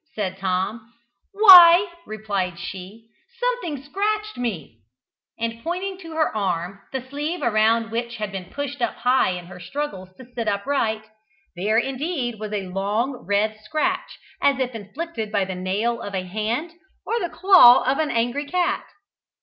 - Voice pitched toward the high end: Yes, high, 230 Hz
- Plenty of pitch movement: Yes, wide, 6.6 semitones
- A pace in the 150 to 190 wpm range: Yes, average, 160 wpm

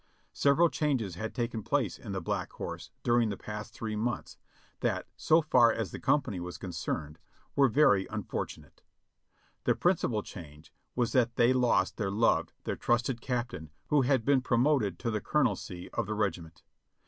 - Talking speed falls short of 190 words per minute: Yes, average, 165 wpm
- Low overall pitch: Yes, low, 115 Hz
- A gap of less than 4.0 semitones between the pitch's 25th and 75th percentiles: No, average, 4.5 semitones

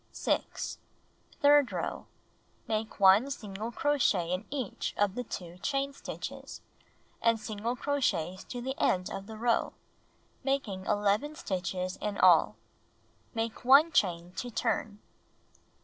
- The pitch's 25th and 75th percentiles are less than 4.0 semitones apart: No, average, 5.3 semitones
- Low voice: No, high, 220 Hz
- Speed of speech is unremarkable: No, slow, 125 wpm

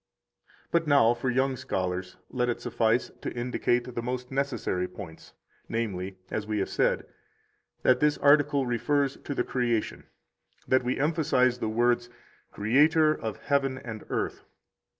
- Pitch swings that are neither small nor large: Yes, average, 3.5 semitones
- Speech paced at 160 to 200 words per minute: No, average, 145 wpm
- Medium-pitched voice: No, low, 125 Hz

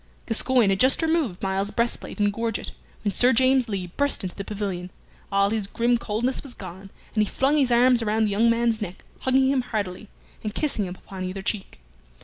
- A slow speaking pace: No, average, 200 wpm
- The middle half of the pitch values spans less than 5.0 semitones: Yes, average, 3.9 semitones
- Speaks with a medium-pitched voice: No, high, 220 Hz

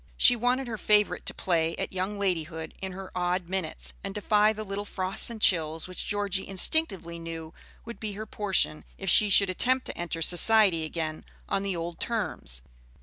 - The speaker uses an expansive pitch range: No, average, 3.7 semitones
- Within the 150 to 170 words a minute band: No, average, 185 wpm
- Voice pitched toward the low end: No, high, 190 Hz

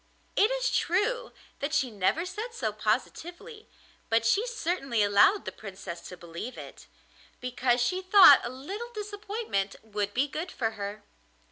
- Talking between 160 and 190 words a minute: No, average, 150 wpm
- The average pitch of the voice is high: Yes, very high, 275 Hz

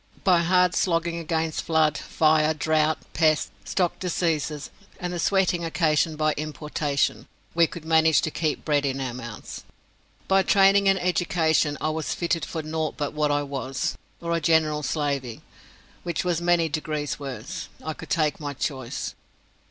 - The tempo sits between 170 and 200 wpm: No, average, 160 wpm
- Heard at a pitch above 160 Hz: No, medium, 155 Hz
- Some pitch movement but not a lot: No, narrow, 2.3 semitones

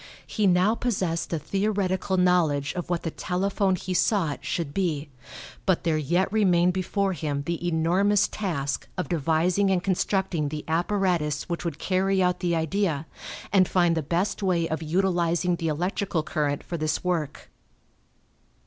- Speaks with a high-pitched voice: No, medium, 175 Hz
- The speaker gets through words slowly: No, average, 155 wpm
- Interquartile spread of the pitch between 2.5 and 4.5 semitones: Yes, average, 2.9 semitones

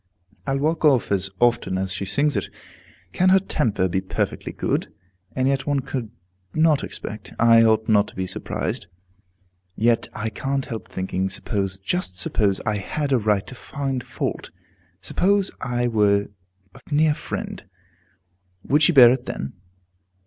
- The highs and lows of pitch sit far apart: Yes, wide, 5.9 semitones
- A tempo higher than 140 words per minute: Yes, average, 155 wpm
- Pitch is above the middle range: No, low, 120 Hz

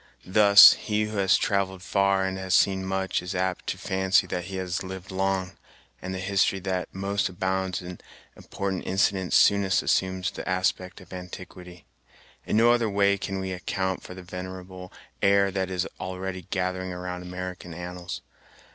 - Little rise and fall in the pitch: Yes, narrow, 1.0 semitones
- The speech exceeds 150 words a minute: Yes, average, 165 wpm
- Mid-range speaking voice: No, very low, 95 Hz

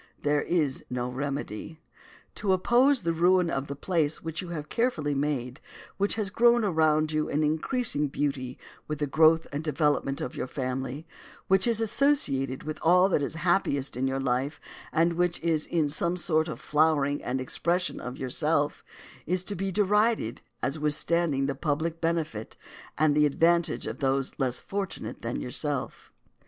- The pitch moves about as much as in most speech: Yes, average, 3.9 semitones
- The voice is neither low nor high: Yes, medium, 155 Hz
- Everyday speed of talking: Yes, average, 165 wpm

